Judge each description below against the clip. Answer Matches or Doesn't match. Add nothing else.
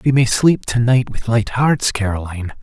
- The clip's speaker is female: Doesn't match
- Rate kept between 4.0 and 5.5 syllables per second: Matches